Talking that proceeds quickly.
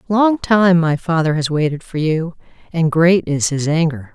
No: average, 190 wpm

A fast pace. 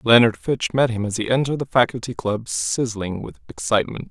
No: average, 190 wpm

